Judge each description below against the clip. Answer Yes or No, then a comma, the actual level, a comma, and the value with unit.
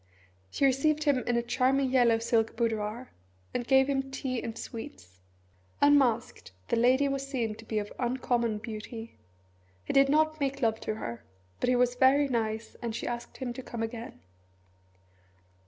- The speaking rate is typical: Yes, average, 170 wpm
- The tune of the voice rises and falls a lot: No, average, 3.1 semitones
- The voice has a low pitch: No, high, 245 Hz